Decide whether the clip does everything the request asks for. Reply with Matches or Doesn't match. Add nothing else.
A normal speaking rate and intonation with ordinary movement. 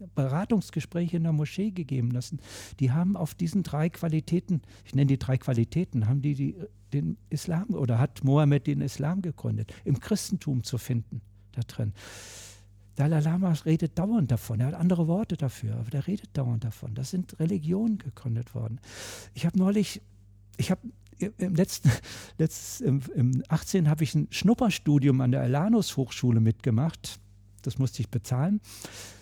Doesn't match